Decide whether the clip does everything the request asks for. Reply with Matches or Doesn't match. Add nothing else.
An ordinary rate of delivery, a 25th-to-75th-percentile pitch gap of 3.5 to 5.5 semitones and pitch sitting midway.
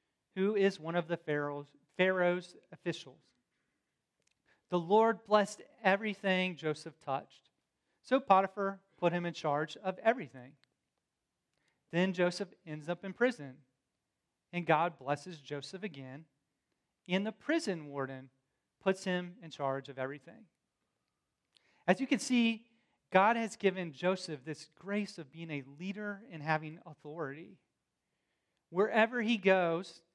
Doesn't match